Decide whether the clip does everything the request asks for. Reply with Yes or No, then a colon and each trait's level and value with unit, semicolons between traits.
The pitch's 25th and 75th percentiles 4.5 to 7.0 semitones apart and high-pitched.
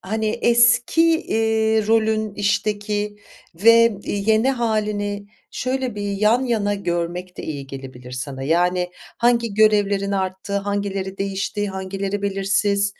No: narrow, 2.4 semitones; high, 205 Hz